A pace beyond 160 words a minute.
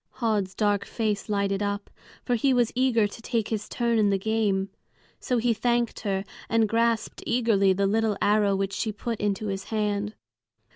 Yes: average, 180 wpm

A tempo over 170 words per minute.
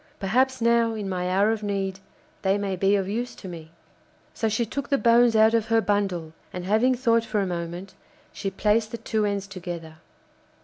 Yes: average, 200 wpm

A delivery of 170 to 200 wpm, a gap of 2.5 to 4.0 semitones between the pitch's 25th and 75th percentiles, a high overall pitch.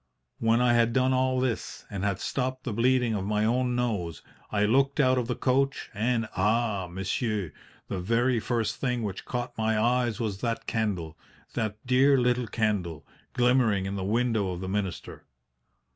No: average, 175 wpm; average, 3.3 semitones; low, 115 Hz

